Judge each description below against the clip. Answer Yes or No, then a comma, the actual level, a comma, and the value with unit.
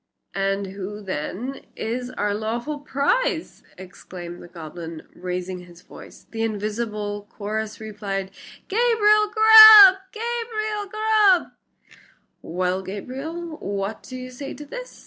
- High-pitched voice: Yes, high, 225 Hz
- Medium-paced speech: No, slow, 115 wpm